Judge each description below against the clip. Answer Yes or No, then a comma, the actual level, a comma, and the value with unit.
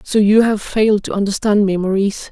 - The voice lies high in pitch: Yes, high, 205 Hz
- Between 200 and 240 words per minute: Yes, fast, 205 wpm